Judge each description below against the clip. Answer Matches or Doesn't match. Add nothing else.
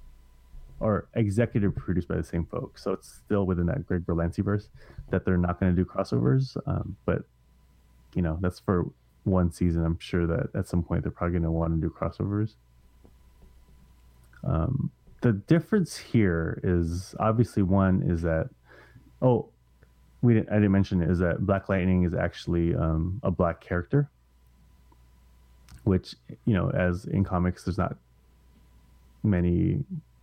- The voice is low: Matches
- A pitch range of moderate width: Doesn't match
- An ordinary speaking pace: Matches